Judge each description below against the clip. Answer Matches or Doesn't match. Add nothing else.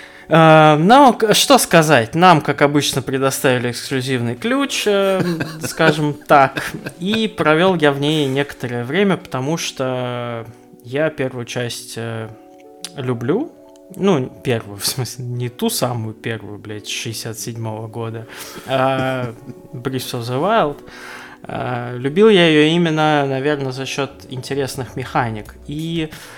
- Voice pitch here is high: Doesn't match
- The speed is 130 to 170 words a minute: Doesn't match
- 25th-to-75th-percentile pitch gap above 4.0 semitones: Matches